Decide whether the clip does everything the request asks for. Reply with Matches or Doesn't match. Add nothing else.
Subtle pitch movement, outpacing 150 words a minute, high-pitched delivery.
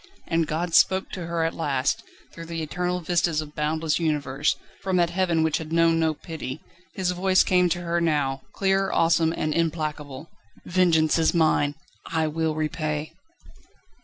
Doesn't match